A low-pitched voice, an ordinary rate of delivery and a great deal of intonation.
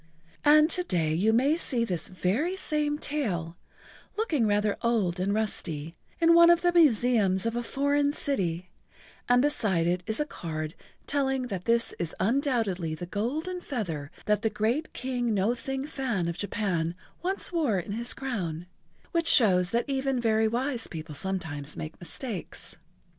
No: high, 225 Hz; average, 160 wpm; wide, 7.3 semitones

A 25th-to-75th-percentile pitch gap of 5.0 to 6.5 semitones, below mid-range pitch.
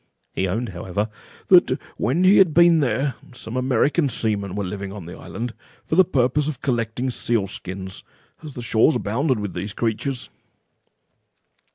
Yes: average, 5.3 semitones; low, 120 Hz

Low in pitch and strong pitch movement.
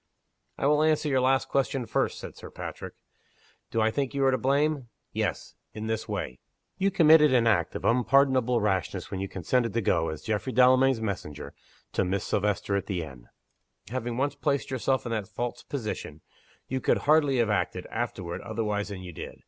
No: low, 120 Hz; average, 4.8 semitones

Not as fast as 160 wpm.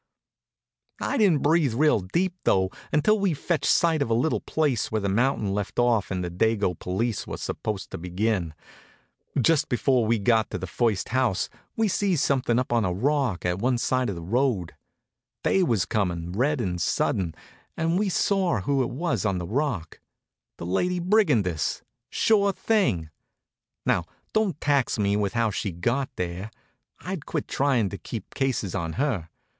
No: average, 170 wpm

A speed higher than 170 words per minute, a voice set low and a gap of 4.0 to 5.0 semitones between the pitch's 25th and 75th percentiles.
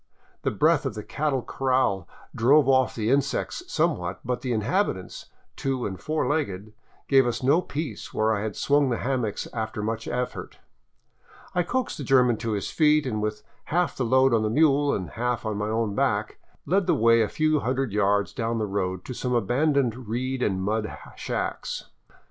Yes: average, 185 wpm; low, 125 Hz; average, 4.4 semitones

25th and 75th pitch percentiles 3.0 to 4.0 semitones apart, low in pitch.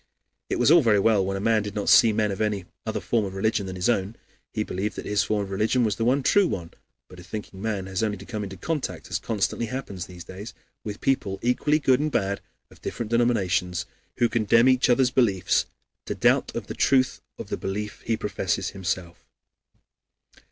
Yes: average, 3.5 semitones; low, 105 Hz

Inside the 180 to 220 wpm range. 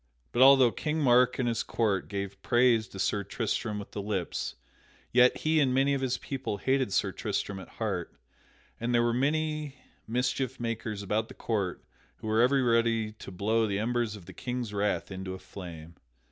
Yes: average, 190 wpm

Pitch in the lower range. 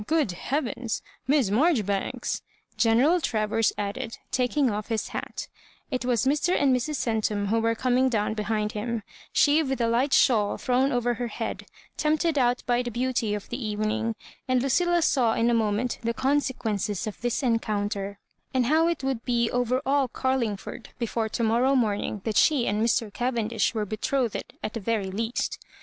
No: high, 235 Hz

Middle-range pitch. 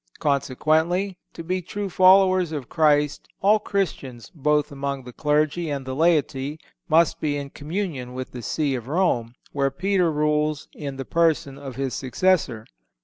Yes: medium, 150 Hz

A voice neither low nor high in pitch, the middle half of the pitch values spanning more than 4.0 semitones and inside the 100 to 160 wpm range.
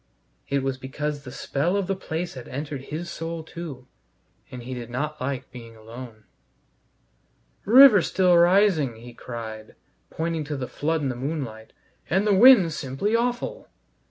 Yes: medium, 145 Hz; wide, 5.4 semitones; average, 155 wpm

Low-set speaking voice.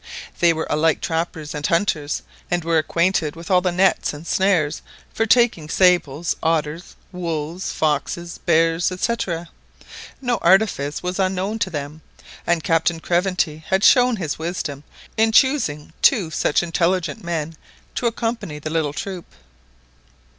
No: medium, 170 Hz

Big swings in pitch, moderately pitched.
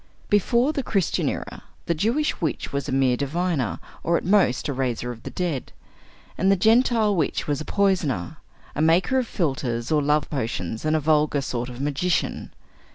Yes: wide, 6.3 semitones; medium, 155 Hz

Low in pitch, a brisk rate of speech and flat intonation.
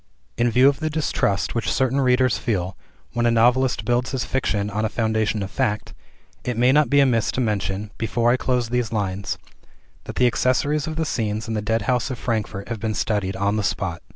No: low, 115 Hz; fast, 210 wpm; average, 3.3 semitones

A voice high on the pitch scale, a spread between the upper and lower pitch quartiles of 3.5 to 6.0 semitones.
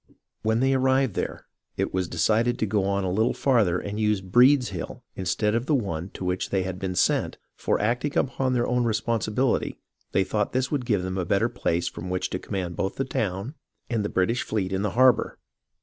No: low, 105 Hz; average, 4.7 semitones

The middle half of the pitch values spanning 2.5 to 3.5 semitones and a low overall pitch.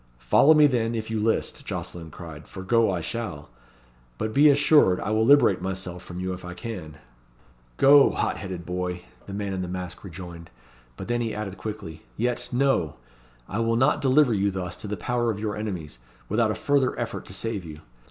No: average, 4.7 semitones; low, 105 Hz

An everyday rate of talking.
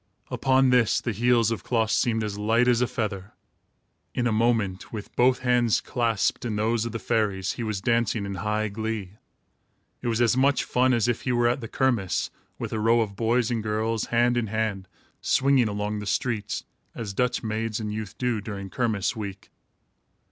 Yes: average, 190 wpm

